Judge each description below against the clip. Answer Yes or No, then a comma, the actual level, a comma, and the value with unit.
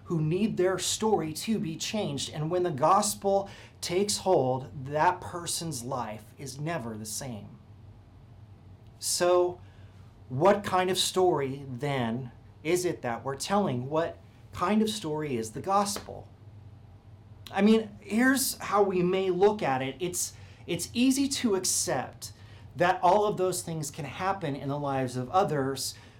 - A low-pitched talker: No, medium, 150 Hz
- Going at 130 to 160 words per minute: Yes, average, 145 wpm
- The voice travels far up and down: Yes, wide, 8.4 semitones